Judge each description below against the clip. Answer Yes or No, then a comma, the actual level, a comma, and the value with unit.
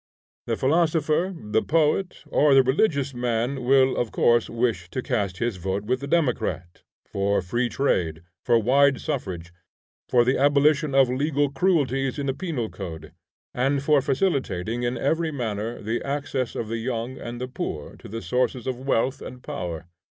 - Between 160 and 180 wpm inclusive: Yes, average, 165 wpm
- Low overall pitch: Yes, low, 125 Hz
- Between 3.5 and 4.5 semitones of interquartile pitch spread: Yes, average, 3.9 semitones